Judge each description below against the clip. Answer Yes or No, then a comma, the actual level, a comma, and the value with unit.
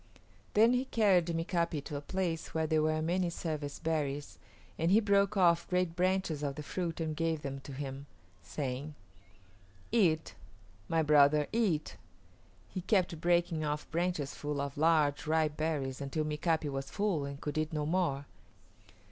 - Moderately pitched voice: Yes, medium, 160 Hz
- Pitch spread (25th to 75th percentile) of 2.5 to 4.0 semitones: Yes, average, 3.1 semitones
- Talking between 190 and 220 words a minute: No, average, 160 wpm